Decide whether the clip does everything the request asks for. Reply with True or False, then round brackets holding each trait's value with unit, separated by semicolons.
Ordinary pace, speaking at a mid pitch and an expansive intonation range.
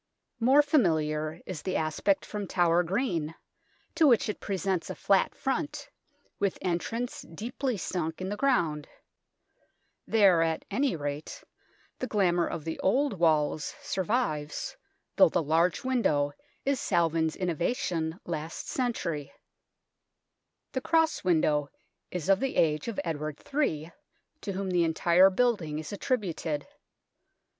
False (130 wpm; 175 Hz; 6.1 semitones)